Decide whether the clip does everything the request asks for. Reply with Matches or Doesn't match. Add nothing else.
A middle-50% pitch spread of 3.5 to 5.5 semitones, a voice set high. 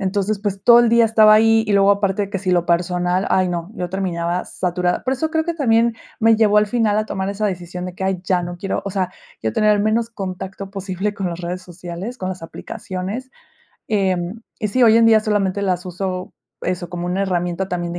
Doesn't match